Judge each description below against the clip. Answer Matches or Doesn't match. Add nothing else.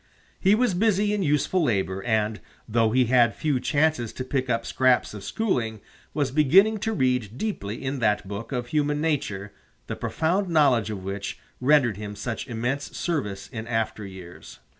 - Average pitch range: Doesn't match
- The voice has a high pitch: Doesn't match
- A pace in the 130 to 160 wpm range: Doesn't match